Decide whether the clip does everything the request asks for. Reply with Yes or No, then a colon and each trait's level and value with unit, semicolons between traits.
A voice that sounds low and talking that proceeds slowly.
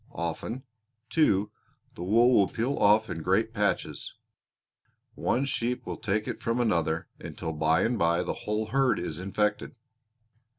No: low, 105 Hz; average, 145 wpm